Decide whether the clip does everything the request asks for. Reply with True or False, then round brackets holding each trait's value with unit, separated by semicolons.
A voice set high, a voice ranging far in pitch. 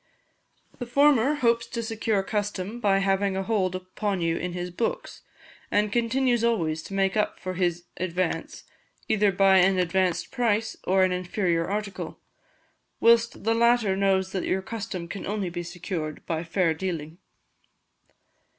False (195 Hz; 3.7 semitones)